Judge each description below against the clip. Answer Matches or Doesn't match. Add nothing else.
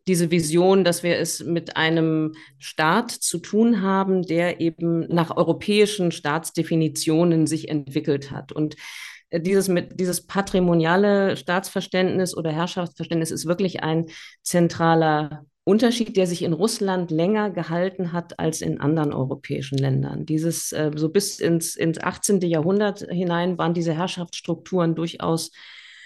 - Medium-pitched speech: Matches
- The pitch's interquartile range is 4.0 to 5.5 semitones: Doesn't match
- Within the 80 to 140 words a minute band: Matches